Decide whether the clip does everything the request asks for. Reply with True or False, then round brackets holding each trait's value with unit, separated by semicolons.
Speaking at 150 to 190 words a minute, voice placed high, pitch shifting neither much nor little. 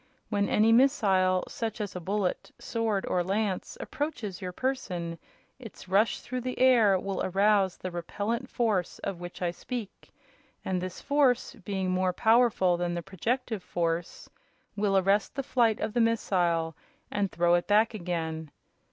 True (155 wpm; 195 Hz; 4.1 semitones)